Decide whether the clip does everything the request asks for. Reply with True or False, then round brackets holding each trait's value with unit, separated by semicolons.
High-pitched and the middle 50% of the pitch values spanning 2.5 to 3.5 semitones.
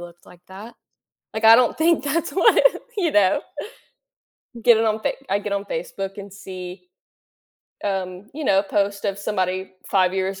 True (200 Hz; 3.1 semitones)